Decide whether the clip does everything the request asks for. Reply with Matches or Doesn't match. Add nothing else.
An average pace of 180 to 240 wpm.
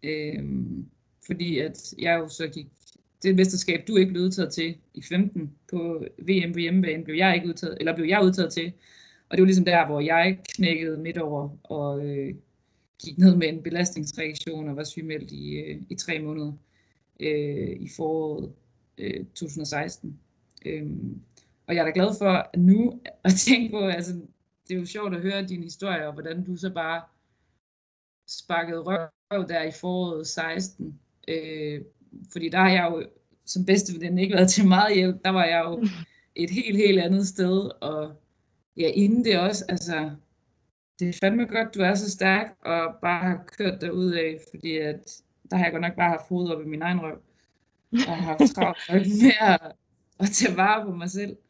Matches